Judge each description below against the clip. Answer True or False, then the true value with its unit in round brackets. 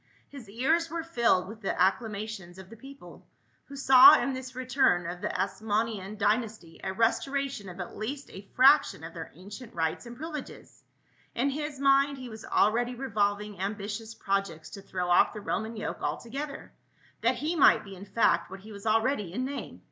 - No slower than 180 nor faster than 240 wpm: True (185 wpm)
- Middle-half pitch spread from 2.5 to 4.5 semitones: False (5.3 semitones)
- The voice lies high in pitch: True (220 Hz)